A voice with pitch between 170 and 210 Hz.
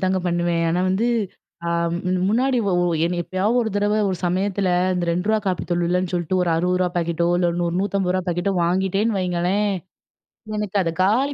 Yes: medium, 185 Hz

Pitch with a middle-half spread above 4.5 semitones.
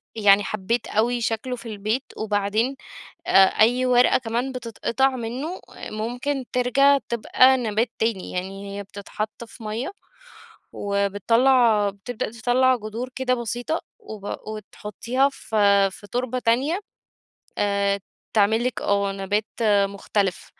No: average, 3.6 semitones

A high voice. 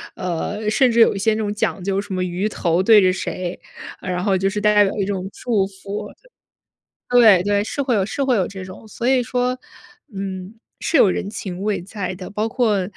Yes: high, 200 Hz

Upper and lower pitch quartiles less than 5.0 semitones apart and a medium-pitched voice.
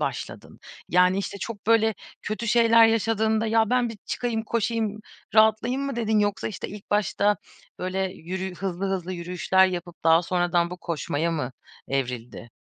No: average, 3.9 semitones; high, 200 Hz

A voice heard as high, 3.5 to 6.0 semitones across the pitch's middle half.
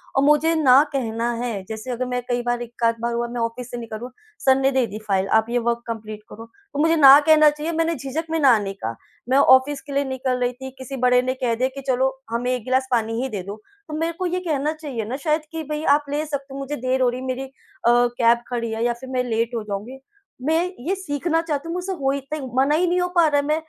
Yes: very high, 260 Hz; average, 3.9 semitones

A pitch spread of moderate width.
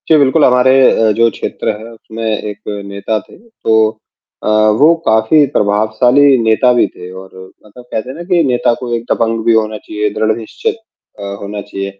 Yes: average, 3.0 semitones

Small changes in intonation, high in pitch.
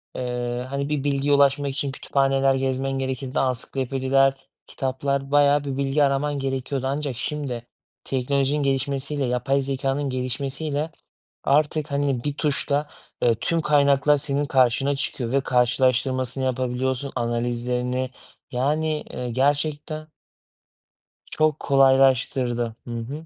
No: narrow, 1.8 semitones; low, 135 Hz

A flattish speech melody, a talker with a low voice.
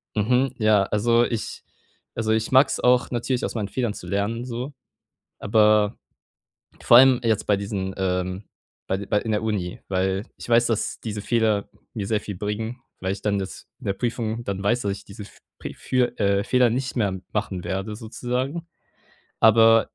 No: average, 3.0 semitones; low, 110 Hz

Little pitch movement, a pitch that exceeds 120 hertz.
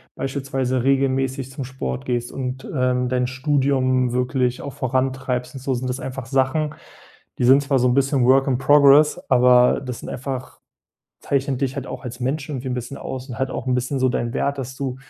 Yes: narrow, 1.4 semitones; low, 130 Hz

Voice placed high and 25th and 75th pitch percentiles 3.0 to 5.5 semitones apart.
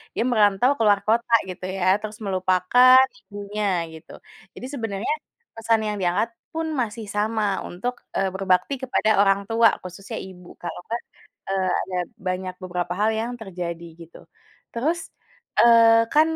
Yes: high, 210 Hz; average, 3.7 semitones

